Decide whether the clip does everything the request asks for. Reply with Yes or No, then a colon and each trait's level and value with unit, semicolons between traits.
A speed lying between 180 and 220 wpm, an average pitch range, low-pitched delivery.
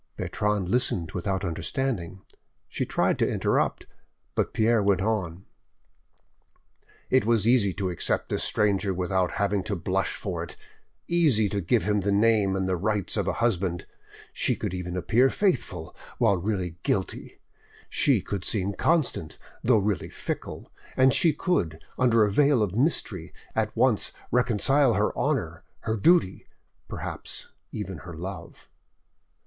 No: average, 145 wpm; average, 3.9 semitones; low, 100 Hz